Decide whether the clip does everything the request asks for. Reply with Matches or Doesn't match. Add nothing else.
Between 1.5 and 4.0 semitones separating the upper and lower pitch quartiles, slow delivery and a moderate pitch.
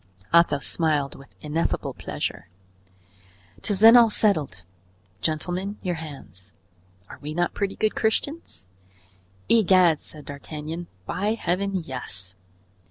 Doesn't match